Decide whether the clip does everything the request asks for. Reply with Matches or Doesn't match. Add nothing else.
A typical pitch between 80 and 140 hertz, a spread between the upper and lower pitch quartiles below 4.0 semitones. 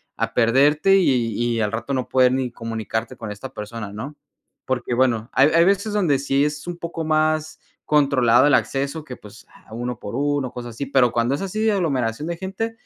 Doesn't match